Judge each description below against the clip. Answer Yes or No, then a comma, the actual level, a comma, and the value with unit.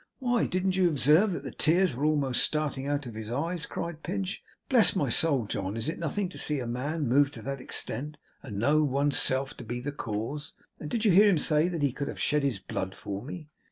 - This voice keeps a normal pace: No, fast, 235 wpm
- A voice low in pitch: No, medium, 145 Hz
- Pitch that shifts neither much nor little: Yes, average, 4.6 semitones